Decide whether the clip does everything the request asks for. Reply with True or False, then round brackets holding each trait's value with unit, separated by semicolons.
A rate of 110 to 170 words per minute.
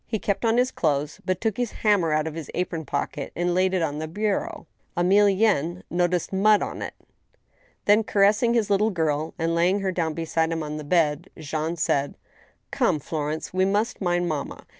False (190 wpm)